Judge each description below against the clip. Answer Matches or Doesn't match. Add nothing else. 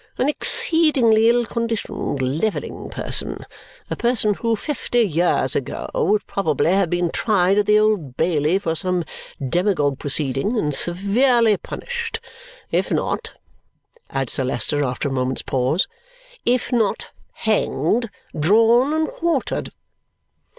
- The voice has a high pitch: Matches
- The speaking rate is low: Matches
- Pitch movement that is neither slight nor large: Doesn't match